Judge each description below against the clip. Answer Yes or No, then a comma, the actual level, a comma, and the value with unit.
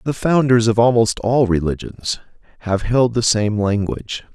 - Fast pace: No, average, 150 wpm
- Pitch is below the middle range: Yes, low, 115 Hz